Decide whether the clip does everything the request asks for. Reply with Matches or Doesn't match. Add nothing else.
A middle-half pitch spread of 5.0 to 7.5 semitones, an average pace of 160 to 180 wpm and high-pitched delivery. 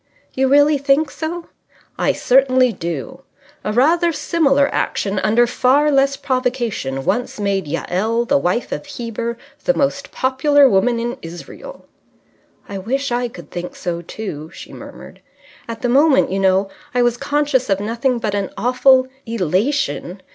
Doesn't match